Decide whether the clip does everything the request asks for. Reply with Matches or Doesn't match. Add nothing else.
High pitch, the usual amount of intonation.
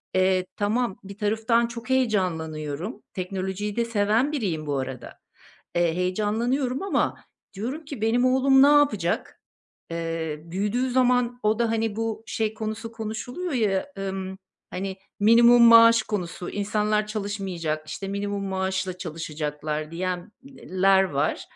Matches